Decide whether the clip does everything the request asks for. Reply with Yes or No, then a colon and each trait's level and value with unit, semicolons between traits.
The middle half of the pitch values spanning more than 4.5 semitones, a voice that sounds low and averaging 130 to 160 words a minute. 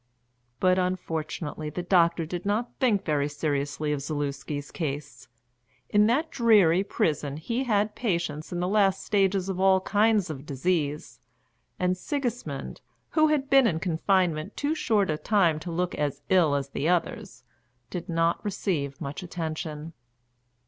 No: average, 4.9 semitones; medium, 175 Hz; average, 150 wpm